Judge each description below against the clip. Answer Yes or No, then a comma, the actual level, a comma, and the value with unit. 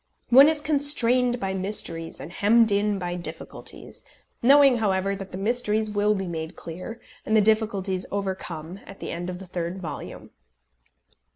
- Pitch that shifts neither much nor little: Yes, average, 3.9 semitones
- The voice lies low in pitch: No, high, 200 Hz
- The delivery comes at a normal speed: Yes, average, 160 wpm